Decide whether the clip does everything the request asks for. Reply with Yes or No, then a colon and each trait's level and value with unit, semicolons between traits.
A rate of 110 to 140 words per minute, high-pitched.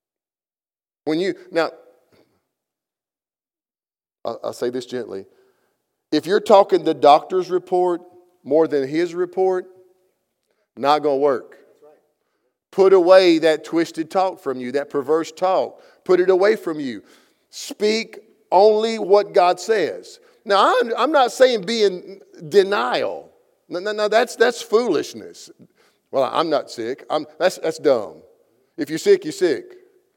Yes: slow, 135 wpm; high, 205 Hz